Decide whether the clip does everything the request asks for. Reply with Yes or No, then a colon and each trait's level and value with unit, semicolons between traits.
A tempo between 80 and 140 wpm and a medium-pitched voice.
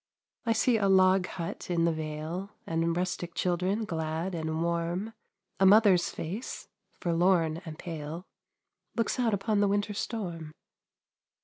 Yes: slow, 135 wpm; medium, 180 Hz